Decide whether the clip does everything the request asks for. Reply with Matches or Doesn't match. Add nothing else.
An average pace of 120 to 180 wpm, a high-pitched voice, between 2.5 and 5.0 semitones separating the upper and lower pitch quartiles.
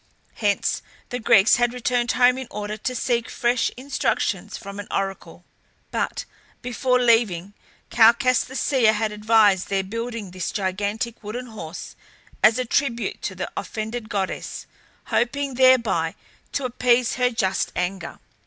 Matches